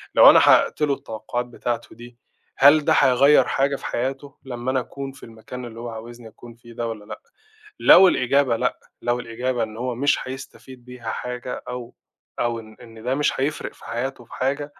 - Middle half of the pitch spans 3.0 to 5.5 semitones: No, narrow, 2.4 semitones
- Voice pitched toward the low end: Yes, low, 125 Hz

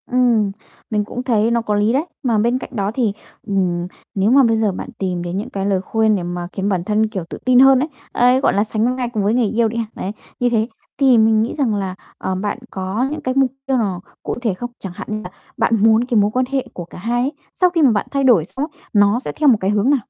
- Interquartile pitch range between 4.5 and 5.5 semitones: No, average, 3.8 semitones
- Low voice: No, high, 220 Hz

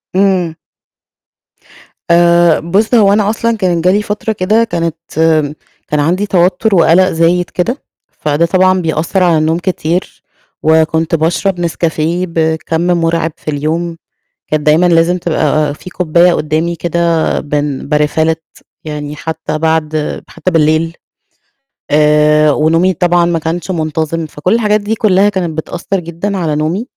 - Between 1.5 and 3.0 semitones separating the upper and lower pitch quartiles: Yes, narrow, 2.6 semitones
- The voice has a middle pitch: Yes, medium, 170 Hz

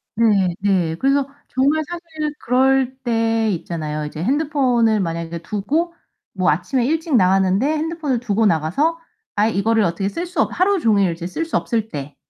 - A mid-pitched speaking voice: No, high, 225 Hz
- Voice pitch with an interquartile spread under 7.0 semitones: No, wide, 7.7 semitones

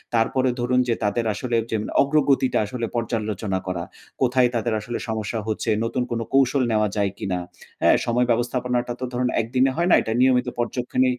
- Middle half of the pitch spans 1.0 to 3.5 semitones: Yes, narrow, 2.5 semitones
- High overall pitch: No, low, 120 Hz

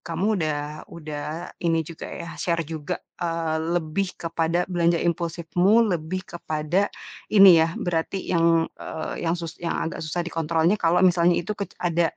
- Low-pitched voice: No, medium, 170 Hz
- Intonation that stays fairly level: Yes, narrow, 1.5 semitones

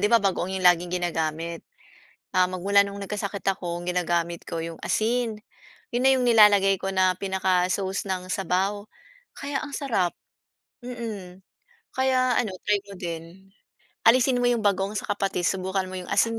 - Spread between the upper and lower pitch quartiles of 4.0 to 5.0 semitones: No, average, 3.2 semitones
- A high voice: Yes, high, 195 Hz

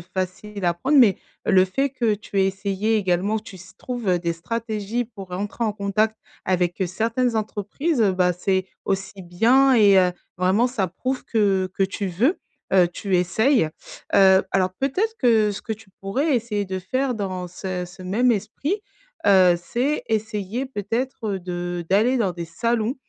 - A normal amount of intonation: Yes, average, 3.8 semitones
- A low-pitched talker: No, high, 200 Hz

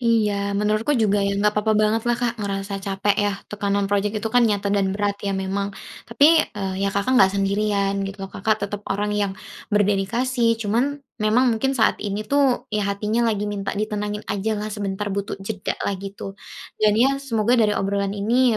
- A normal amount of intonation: No, narrow, 1.8 semitones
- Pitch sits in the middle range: No, high, 205 Hz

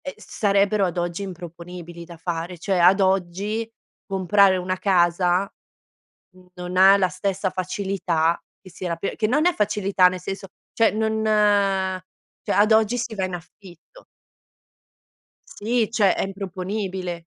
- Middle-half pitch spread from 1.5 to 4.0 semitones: Yes, narrow, 2.4 semitones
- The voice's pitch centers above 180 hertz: Yes, high, 190 Hz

